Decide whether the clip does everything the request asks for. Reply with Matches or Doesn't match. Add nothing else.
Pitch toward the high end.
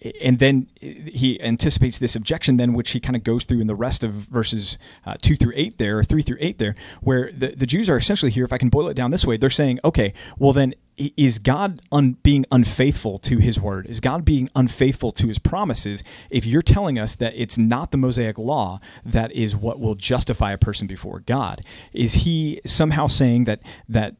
Doesn't match